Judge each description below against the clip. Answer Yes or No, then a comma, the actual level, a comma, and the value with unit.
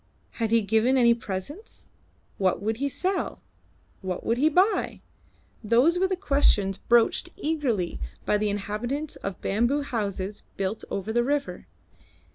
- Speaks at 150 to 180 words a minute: No, average, 140 wpm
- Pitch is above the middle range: Yes, high, 230 Hz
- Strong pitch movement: Yes, wide, 5.9 semitones